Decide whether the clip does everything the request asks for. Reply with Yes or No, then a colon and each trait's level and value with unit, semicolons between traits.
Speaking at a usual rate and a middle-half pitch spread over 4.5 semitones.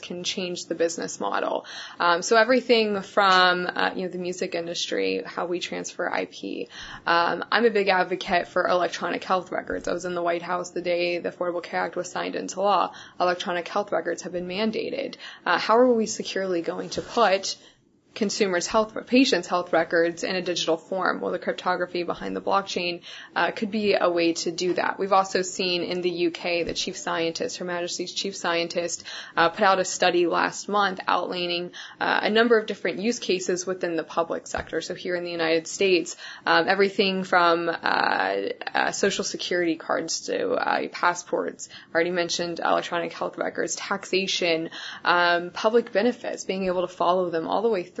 No: average, 185 wpm; narrow, 2.4 semitones